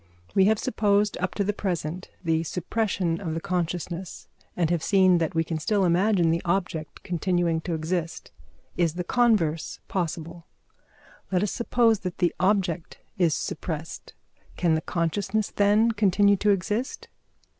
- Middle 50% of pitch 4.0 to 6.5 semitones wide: No, average, 3.4 semitones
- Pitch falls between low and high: Yes, medium, 180 Hz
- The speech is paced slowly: No, average, 150 wpm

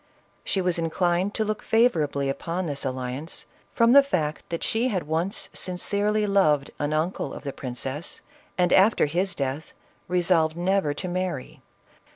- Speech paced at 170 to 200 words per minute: No, average, 160 wpm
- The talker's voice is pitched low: No, medium, 175 Hz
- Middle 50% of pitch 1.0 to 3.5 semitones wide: No, average, 4.7 semitones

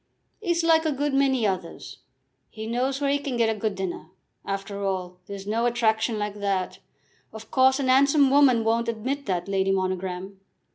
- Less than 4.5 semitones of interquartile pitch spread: No, wide, 5.5 semitones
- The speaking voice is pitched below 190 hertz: No, high, 225 Hz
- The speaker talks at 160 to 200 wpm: Yes, average, 180 wpm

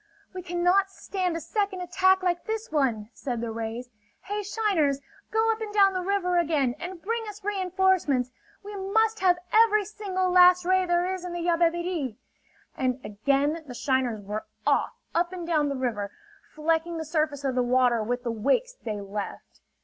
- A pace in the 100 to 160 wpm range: No, average, 180 wpm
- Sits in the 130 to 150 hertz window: No, very high, 345 Hz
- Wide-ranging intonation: Yes, wide, 6.5 semitones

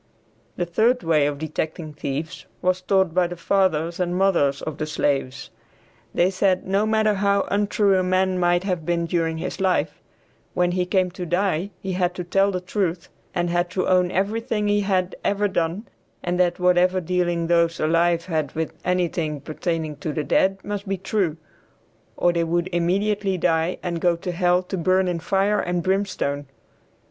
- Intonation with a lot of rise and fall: No, narrow, 2.4 semitones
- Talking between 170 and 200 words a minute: Yes, average, 175 wpm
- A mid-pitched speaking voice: Yes, medium, 180 Hz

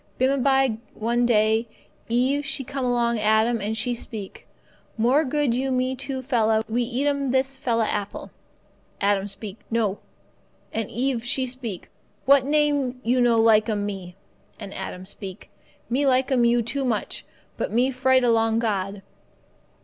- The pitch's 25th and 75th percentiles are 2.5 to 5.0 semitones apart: Yes, average, 3.2 semitones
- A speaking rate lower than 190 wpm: Yes, average, 160 wpm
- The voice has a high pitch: Yes, high, 240 Hz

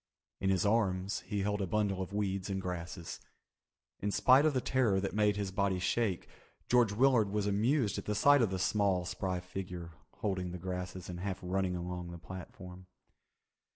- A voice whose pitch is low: Yes, very low, 95 Hz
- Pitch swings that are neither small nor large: No, narrow, 2.3 semitones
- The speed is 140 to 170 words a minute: No, average, 185 wpm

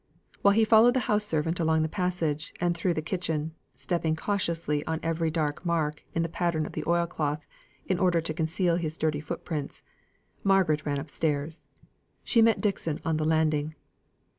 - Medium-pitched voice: Yes, medium, 160 Hz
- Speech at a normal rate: Yes, average, 180 wpm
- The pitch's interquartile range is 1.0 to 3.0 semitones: Yes, narrow, 2.5 semitones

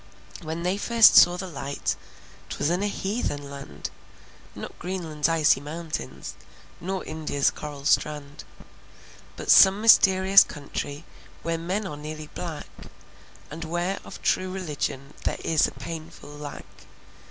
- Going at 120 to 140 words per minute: Yes, slow, 135 wpm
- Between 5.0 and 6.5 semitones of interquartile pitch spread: No, average, 4.0 semitones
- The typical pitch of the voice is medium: Yes, medium, 160 Hz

